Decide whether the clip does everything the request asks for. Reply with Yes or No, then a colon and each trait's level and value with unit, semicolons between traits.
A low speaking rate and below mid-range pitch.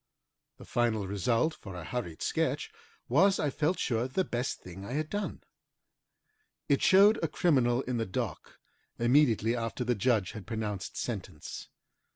No: average, 155 wpm; low, 120 Hz